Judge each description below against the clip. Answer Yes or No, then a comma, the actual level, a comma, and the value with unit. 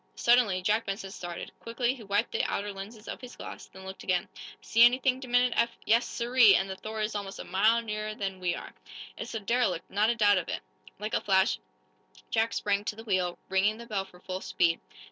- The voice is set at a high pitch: Yes, high, 210 Hz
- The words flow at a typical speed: No, fast, 220 wpm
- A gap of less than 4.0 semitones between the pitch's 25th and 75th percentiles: Yes, average, 3.3 semitones